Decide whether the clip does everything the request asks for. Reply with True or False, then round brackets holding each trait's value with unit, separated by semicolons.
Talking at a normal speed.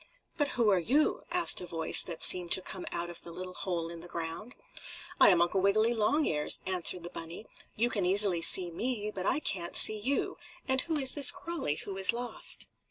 False (210 wpm)